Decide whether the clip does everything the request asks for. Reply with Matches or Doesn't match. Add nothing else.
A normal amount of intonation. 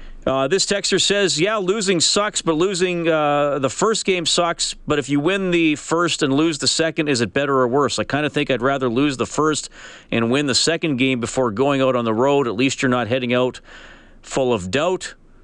Matches